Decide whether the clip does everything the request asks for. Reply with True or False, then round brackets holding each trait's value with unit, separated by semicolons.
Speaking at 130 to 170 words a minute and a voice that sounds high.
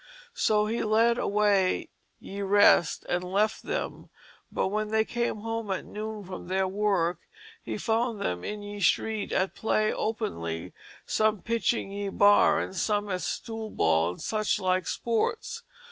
True (150 wpm; 205 Hz)